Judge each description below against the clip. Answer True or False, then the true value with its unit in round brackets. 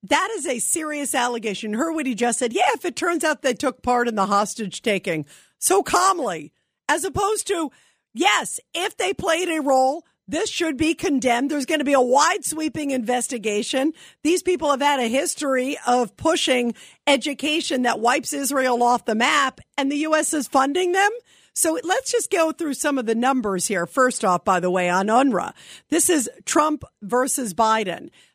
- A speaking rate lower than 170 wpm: False (185 wpm)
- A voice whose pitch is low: False (275 Hz)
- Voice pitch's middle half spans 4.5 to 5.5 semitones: True (4.9 semitones)